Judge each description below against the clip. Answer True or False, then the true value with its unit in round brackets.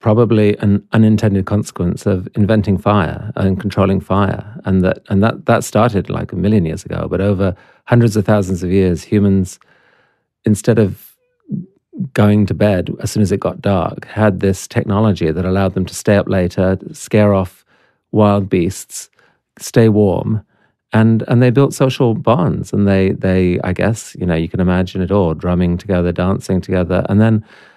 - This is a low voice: True (100 Hz)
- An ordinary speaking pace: True (175 wpm)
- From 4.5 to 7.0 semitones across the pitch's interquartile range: False (2.6 semitones)